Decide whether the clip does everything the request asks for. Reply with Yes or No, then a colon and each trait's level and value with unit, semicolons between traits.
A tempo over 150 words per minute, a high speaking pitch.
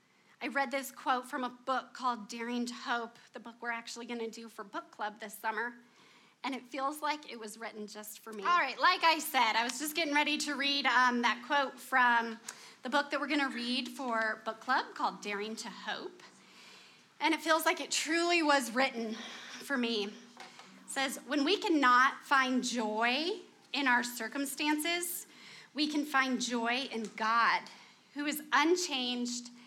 Yes: average, 185 wpm; very high, 255 Hz